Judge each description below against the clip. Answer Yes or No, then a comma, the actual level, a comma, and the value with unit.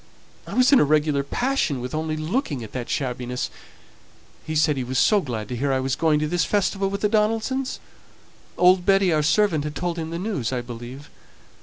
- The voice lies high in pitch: No, medium, 155 Hz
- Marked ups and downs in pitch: Yes, wide, 6.7 semitones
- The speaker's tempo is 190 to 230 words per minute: Yes, fast, 205 wpm